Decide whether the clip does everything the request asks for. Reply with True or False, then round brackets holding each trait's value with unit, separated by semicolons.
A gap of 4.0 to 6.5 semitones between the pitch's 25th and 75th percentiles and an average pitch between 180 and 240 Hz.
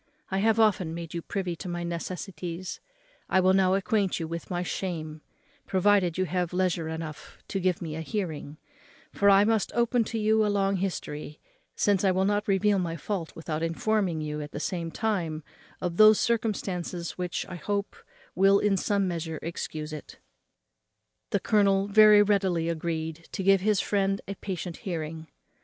False (3.3 semitones; 185 Hz)